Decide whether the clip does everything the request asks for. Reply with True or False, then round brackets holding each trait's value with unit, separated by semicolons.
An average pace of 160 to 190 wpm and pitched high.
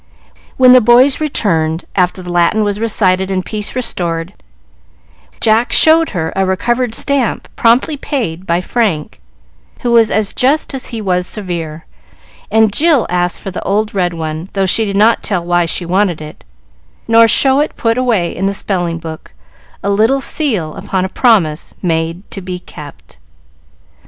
True (165 wpm; 195 Hz)